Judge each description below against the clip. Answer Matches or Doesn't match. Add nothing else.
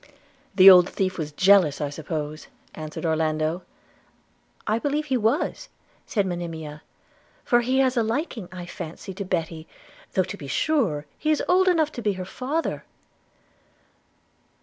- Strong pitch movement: Matches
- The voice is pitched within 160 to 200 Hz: Matches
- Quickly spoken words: Doesn't match